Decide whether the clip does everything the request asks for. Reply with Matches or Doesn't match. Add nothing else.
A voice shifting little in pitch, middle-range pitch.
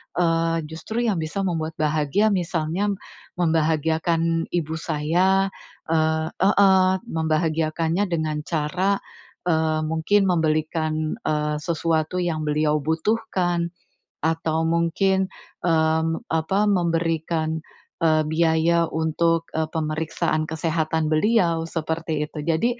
Matches